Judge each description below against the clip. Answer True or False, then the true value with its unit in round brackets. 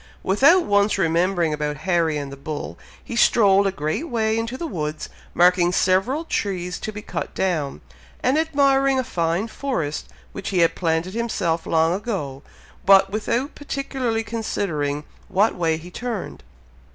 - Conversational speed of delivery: True (150 wpm)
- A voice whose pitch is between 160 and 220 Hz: True (190 Hz)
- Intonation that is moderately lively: False (6.0 semitones)